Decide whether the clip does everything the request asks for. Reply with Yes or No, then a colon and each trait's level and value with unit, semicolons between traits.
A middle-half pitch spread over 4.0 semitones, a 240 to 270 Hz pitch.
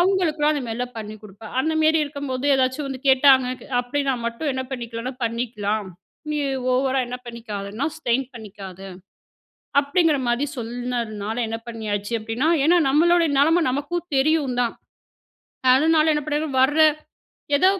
Yes: average, 4.4 semitones; very high, 260 Hz